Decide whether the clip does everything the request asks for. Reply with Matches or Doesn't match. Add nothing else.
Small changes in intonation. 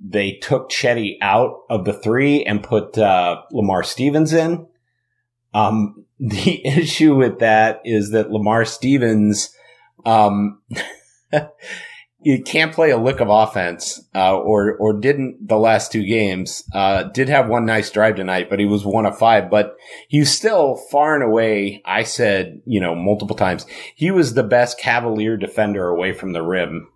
Doesn't match